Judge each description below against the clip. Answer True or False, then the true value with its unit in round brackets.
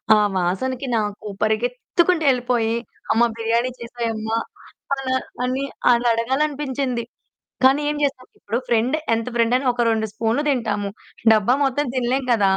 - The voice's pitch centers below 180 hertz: False (240 Hz)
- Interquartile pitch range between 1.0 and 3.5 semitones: True (2.7 semitones)